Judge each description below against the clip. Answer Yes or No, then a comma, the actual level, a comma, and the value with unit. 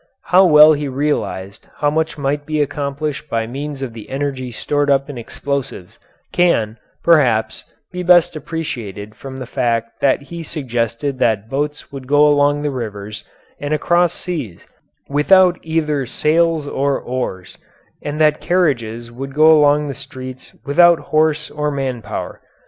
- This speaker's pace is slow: No, average, 150 wpm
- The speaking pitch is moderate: Yes, medium, 145 Hz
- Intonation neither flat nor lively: Yes, average, 3.4 semitones